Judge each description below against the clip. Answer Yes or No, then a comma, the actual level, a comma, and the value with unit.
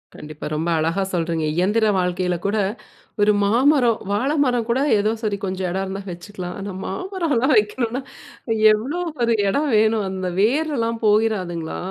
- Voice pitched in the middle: No, high, 210 Hz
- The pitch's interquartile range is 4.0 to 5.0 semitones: Yes, average, 4.4 semitones